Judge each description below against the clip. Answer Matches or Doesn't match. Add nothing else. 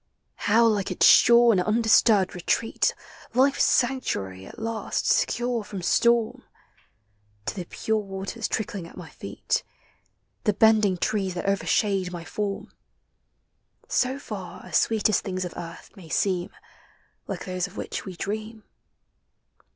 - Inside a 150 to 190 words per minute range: Doesn't match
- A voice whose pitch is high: Matches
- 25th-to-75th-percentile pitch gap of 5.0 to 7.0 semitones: Doesn't match